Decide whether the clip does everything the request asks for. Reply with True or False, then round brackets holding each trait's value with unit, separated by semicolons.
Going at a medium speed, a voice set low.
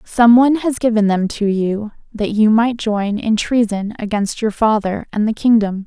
False (195 wpm; 215 Hz)